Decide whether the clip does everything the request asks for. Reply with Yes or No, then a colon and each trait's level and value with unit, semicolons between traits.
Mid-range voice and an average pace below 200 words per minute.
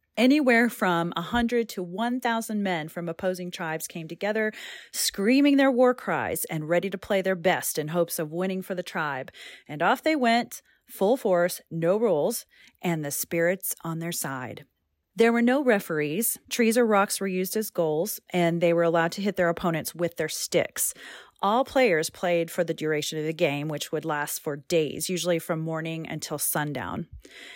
Yes: medium, 180 Hz; average, 185 wpm